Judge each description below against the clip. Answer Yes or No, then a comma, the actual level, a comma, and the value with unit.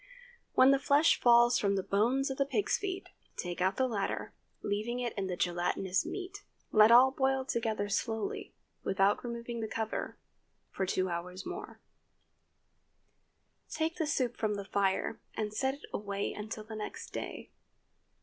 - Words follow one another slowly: No, average, 155 wpm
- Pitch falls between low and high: No, high, 220 Hz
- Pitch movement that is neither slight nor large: Yes, average, 4.9 semitones